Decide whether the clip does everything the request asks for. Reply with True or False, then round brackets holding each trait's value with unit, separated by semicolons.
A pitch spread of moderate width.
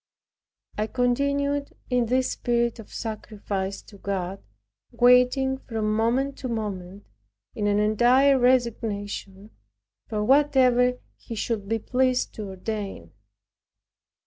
True (3.5 semitones)